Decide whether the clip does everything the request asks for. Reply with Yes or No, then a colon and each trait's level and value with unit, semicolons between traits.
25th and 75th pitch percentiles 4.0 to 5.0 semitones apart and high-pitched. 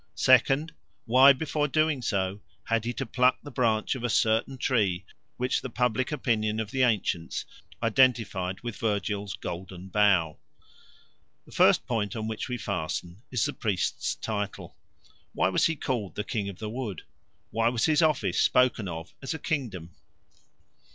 No: average, 4.4 semitones; low, 110 Hz